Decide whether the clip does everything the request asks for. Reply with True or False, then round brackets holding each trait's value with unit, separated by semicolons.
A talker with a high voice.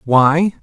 False (150 Hz)